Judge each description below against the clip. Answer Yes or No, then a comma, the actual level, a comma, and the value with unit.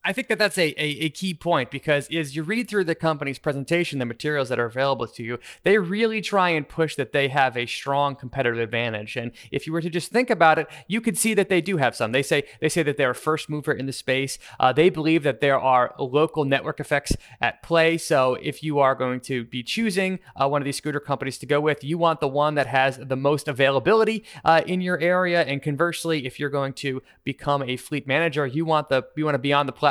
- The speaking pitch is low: No, medium, 150 Hz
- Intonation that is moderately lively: Yes, average, 3.5 semitones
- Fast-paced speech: Yes, fast, 255 wpm